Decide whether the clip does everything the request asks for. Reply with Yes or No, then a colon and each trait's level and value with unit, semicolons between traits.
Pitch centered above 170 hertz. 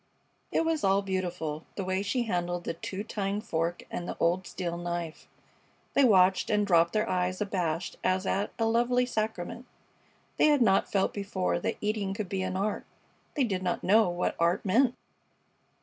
Yes: high, 190 Hz